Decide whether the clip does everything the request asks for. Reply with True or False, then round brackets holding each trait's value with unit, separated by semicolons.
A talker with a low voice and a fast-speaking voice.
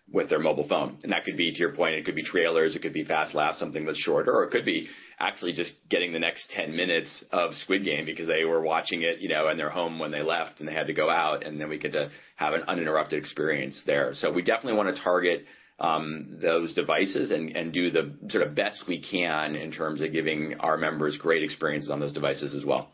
True (80 Hz; 250 wpm)